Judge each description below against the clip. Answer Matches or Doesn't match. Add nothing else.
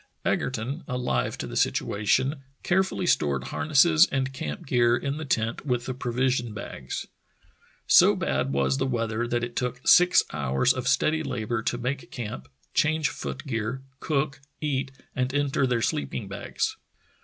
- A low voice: Matches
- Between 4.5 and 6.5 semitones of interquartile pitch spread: Doesn't match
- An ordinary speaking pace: Matches